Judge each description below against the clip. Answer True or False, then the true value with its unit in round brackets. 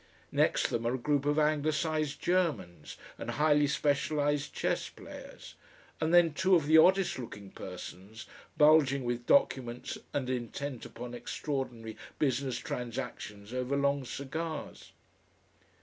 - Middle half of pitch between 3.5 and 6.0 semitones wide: True (4.0 semitones)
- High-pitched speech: False (140 Hz)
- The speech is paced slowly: True (125 wpm)